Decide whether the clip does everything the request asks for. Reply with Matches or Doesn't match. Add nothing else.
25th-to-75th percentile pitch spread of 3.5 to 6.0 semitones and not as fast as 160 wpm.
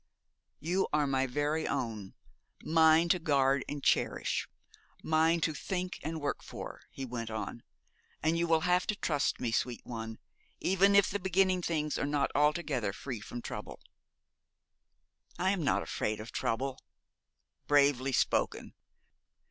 Matches